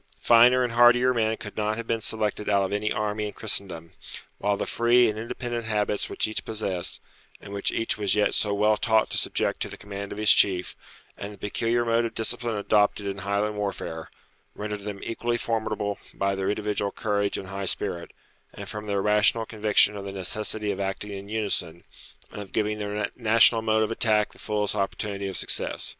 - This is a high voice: No, low, 105 Hz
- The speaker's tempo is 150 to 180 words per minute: No, average, 200 wpm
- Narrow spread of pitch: Yes, narrow, 1.7 semitones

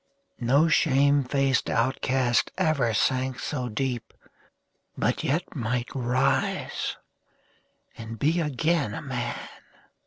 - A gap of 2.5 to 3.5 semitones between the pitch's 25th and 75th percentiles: Yes, average, 2.9 semitones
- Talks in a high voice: No, low, 130 Hz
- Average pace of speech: No, slow, 100 wpm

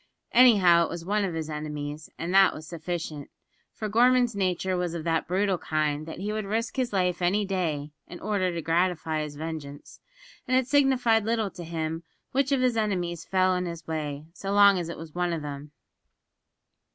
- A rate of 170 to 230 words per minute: Yes, average, 195 wpm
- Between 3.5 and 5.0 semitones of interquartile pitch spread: Yes, average, 4.4 semitones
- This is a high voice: No, medium, 180 Hz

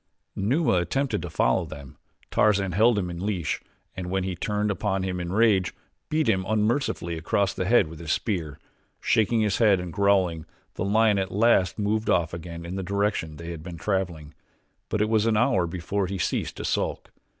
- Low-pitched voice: Yes, very low, 95 Hz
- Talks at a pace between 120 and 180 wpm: No, average, 195 wpm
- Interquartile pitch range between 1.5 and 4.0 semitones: Yes, average, 3.7 semitones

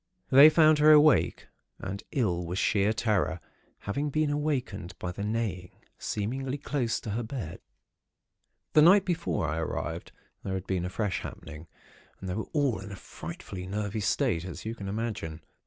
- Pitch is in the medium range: No, low, 105 Hz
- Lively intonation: Yes, wide, 7.1 semitones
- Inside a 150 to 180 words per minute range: Yes, average, 170 wpm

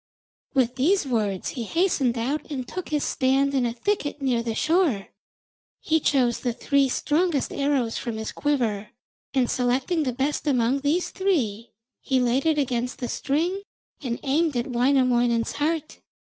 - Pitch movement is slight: No, average, 3.7 semitones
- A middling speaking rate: Yes, average, 160 wpm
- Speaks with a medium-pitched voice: No, very high, 265 Hz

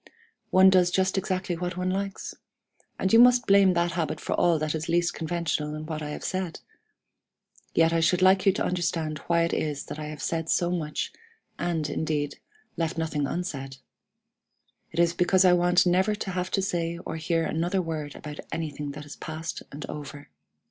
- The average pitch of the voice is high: No, medium, 170 Hz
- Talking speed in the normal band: Yes, average, 190 wpm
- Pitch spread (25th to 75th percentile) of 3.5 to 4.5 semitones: No, average, 2.8 semitones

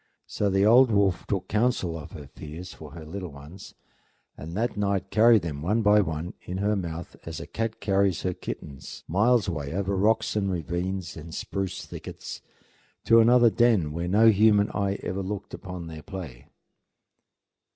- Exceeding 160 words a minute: Yes, average, 170 wpm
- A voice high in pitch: No, very low, 95 Hz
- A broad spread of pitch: No, average, 4.0 semitones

